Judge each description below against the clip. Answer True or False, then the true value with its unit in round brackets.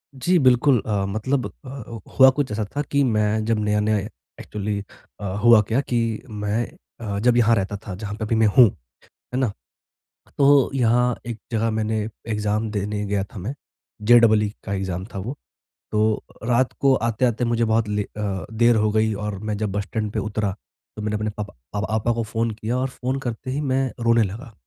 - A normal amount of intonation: False (2.3 semitones)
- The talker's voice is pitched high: False (110 Hz)